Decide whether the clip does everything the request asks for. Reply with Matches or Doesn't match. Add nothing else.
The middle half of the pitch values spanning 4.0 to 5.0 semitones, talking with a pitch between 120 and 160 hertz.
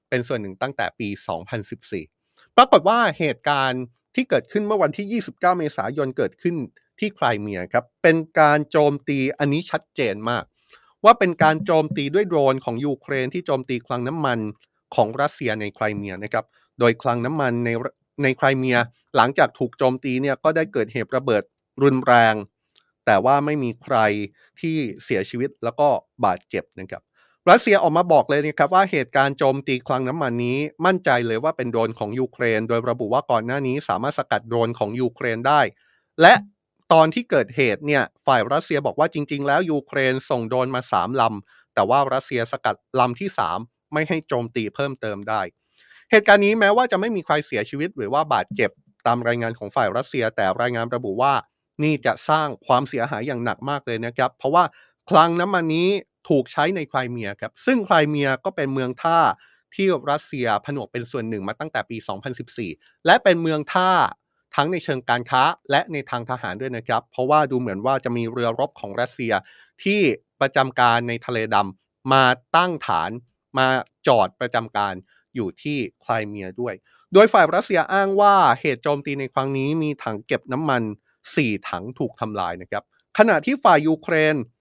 Matches